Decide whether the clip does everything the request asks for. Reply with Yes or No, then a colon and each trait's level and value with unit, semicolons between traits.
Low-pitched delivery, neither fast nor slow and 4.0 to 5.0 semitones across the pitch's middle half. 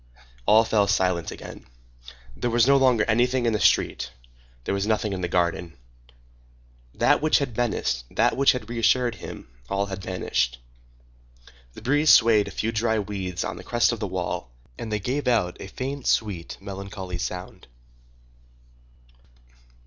Yes: low, 105 Hz; average, 155 wpm; average, 4.4 semitones